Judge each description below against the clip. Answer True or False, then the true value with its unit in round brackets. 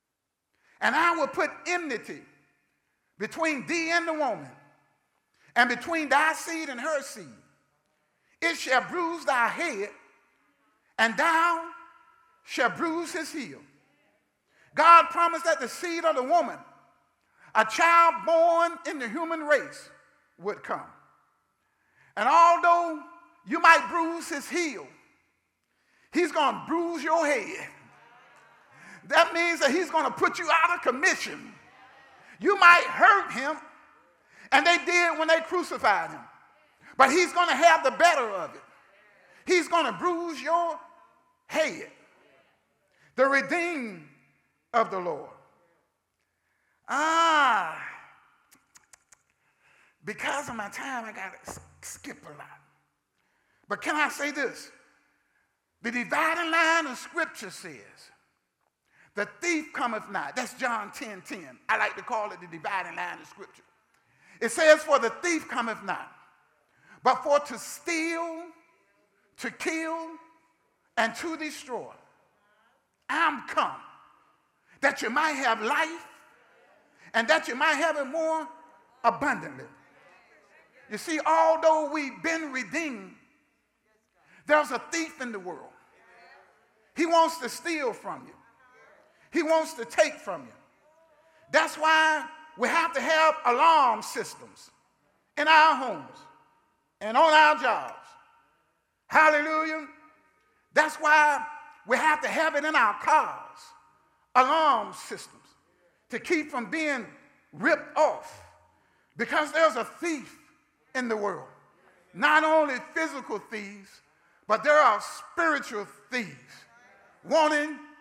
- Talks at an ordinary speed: False (125 wpm)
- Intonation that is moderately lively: True (3.0 semitones)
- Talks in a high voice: True (315 Hz)